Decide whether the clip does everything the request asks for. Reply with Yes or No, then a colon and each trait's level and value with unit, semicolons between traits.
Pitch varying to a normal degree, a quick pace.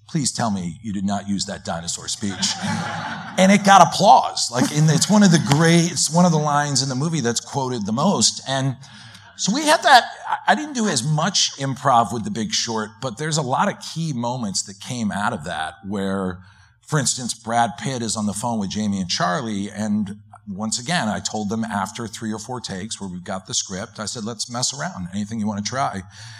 No: wide, 6.7 semitones; fast, 225 wpm